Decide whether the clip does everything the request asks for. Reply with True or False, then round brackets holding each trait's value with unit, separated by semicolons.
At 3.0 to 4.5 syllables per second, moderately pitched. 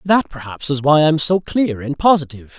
False (5.3 syllables/s; 150 Hz)